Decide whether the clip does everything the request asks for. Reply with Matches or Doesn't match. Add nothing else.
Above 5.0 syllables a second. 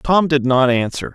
Doesn't match